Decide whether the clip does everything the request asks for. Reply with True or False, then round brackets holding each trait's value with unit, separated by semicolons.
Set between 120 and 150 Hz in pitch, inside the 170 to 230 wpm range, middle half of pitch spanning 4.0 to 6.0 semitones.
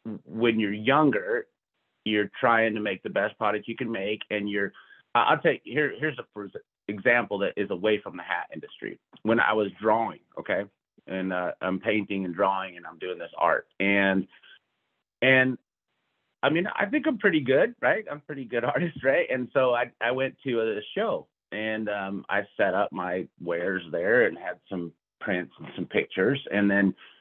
False (110 Hz; 185 wpm; 4.4 semitones)